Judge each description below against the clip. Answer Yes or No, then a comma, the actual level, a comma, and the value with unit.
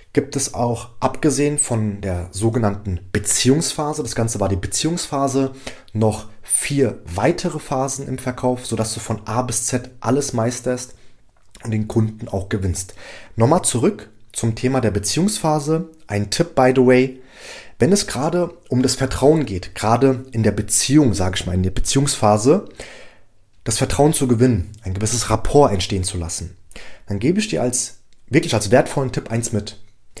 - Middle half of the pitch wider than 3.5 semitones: Yes, average, 4.3 semitones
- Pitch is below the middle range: Yes, low, 120 Hz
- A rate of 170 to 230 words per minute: No, average, 160 wpm